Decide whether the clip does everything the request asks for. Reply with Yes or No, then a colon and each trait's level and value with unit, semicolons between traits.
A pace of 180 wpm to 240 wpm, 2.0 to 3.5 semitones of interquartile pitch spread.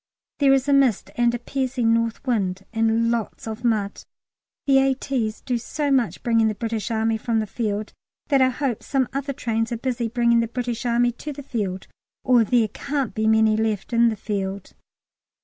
Yes: average, 190 wpm; average, 2.7 semitones